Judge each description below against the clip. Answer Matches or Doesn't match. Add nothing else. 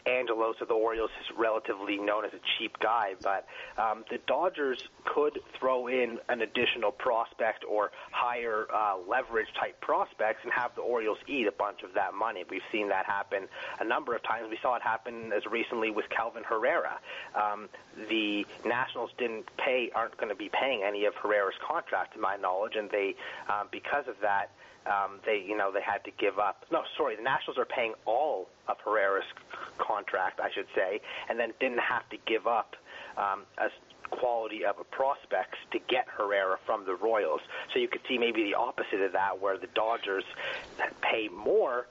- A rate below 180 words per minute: Doesn't match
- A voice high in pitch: Doesn't match